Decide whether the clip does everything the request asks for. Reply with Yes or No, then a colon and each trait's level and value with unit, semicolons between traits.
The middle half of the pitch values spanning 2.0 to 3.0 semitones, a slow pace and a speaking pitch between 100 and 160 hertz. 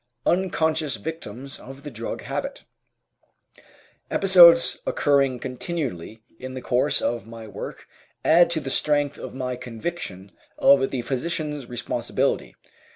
No: average, 4.5 semitones; slow, 120 wpm; low, 135 Hz